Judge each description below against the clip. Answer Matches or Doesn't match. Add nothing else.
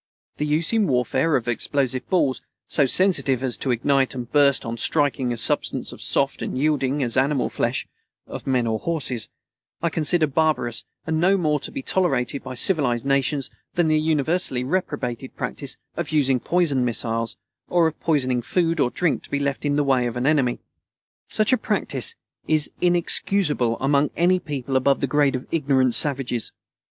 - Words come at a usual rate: Matches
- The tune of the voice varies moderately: Matches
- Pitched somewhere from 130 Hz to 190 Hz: Matches